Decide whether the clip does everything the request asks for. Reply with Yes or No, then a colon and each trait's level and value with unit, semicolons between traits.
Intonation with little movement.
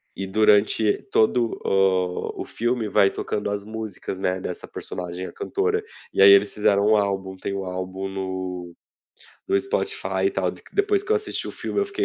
No: average, 4.4 semitones